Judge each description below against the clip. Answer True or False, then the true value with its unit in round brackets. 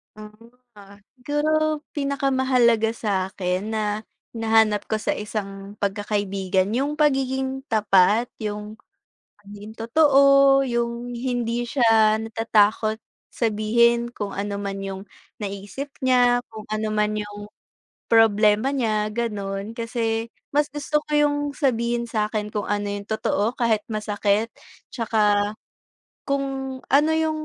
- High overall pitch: True (225 Hz)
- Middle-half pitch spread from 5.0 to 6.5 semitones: False (3.4 semitones)